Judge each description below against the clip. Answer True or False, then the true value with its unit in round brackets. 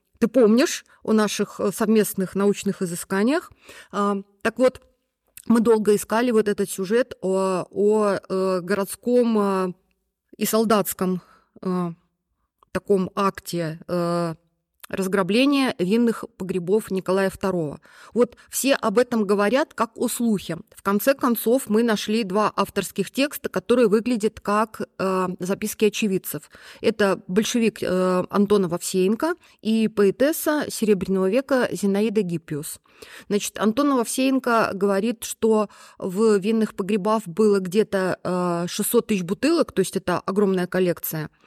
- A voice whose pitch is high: True (205 Hz)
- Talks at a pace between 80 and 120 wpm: True (115 wpm)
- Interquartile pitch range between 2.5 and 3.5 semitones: True (3.0 semitones)